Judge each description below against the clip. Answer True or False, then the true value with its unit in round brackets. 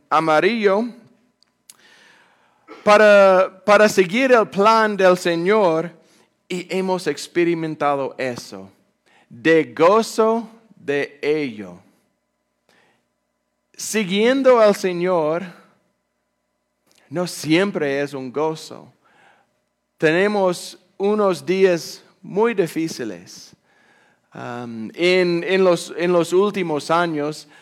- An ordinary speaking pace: False (80 wpm)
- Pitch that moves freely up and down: False (4.4 semitones)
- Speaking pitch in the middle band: True (180 Hz)